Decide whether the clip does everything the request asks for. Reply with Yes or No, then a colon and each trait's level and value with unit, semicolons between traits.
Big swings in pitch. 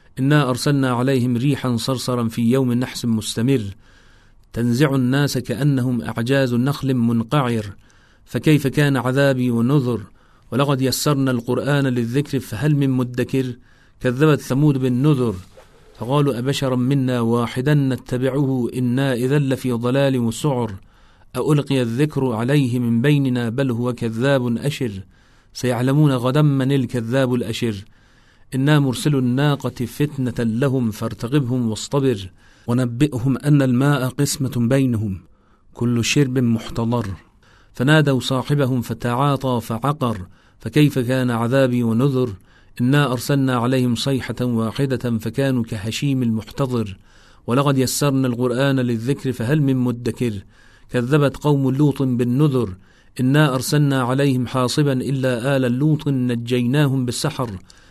No: average, 2.7 semitones